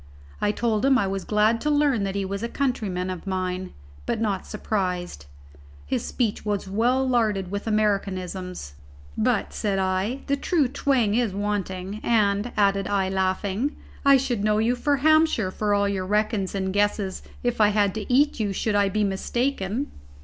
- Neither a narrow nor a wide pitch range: Yes, average, 3.6 semitones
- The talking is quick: No, average, 175 wpm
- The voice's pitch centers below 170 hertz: No, high, 205 Hz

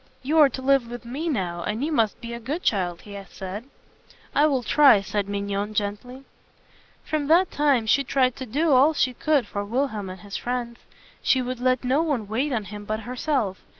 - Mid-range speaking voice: No, high, 245 Hz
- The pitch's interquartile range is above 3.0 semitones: Yes, average, 5.0 semitones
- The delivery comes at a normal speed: No, fast, 210 wpm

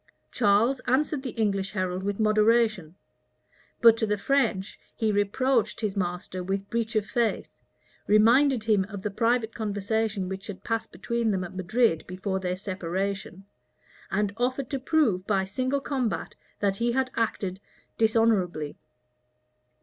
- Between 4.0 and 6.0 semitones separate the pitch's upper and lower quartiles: No, average, 3.4 semitones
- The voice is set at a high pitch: Yes, high, 210 Hz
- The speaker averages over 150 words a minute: No, average, 140 wpm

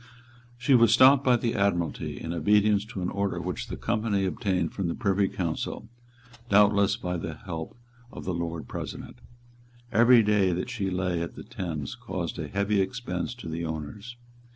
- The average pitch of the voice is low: Yes, low, 100 Hz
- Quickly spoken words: No, average, 175 wpm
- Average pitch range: Yes, average, 4.1 semitones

